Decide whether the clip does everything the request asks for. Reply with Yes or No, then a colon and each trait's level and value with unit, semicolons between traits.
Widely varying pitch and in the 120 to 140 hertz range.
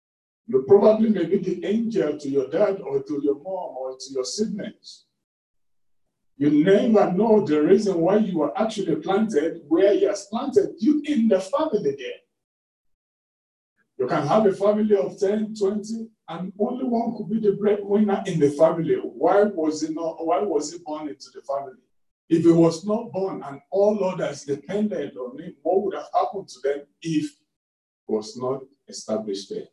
No: wide, 6.1 semitones; high, 190 Hz